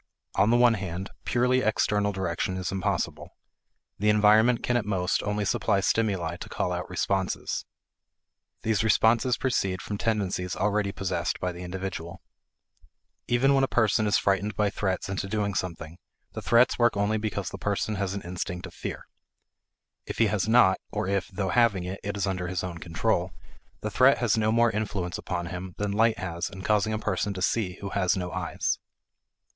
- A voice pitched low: Yes, low, 100 Hz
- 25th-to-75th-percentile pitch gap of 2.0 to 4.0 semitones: Yes, average, 2.9 semitones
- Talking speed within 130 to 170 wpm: No, average, 185 wpm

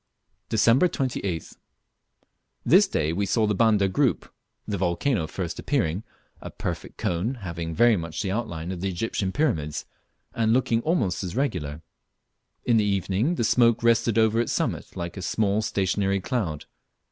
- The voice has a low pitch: Yes, low, 100 Hz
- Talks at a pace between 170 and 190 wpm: No, average, 155 wpm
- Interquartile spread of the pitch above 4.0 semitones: Yes, average, 5.0 semitones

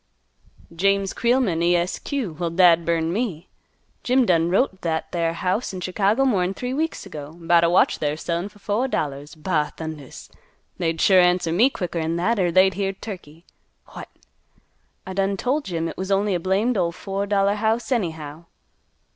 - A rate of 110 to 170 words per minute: No, average, 180 wpm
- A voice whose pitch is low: No, medium, 185 Hz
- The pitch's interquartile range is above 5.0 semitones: No, average, 3.5 semitones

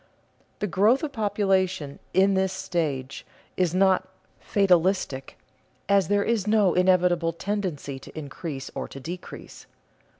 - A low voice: No, medium, 185 Hz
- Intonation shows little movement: No, average, 3.3 semitones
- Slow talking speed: Yes, slow, 125 wpm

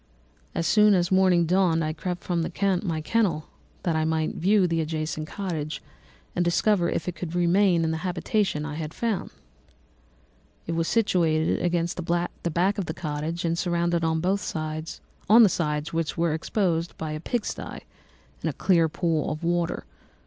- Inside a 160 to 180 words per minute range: Yes, average, 165 wpm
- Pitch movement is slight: Yes, narrow, 2.3 semitones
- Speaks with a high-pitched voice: No, medium, 170 Hz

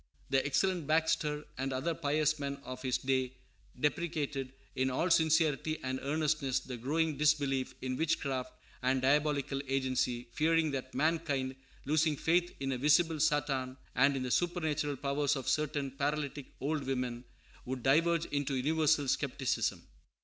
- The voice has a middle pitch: Yes, medium, 145 Hz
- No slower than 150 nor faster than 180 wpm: No, average, 140 wpm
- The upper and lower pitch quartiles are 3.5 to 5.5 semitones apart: No, average, 2.8 semitones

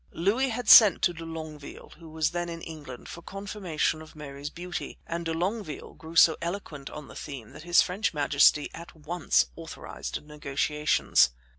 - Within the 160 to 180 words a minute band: Yes, average, 170 wpm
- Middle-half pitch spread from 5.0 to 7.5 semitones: No, average, 2.7 semitones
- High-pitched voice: No, medium, 160 Hz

